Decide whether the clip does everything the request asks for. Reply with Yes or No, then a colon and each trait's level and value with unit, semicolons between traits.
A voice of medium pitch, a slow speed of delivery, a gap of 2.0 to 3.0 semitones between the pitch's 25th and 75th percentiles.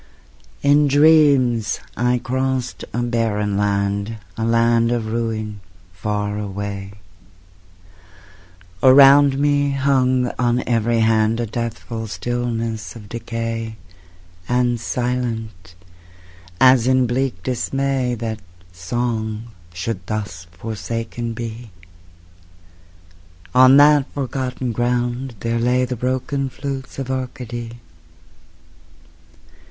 No: low, 120 Hz; slow, 95 wpm; narrow, 2.6 semitones